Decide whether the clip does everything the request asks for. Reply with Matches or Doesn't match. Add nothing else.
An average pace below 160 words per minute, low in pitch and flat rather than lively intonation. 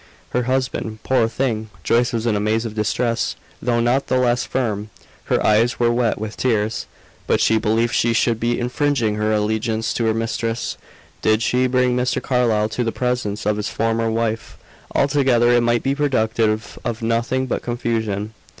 Doesn't match